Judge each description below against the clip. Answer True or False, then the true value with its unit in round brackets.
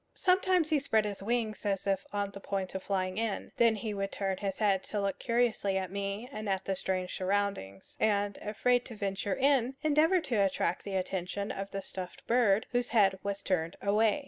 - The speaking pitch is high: True (200 Hz)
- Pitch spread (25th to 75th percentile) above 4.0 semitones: False (3.0 semitones)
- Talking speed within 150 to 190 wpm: False (200 wpm)